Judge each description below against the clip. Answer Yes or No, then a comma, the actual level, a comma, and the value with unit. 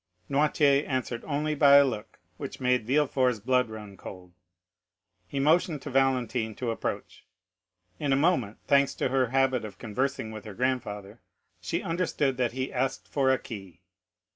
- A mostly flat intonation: No, average, 3.8 semitones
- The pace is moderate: Yes, average, 160 wpm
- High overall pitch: No, low, 130 Hz